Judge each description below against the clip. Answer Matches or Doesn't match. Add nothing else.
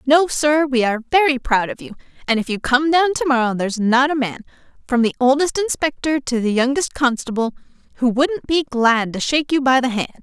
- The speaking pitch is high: Matches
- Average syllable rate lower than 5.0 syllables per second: Doesn't match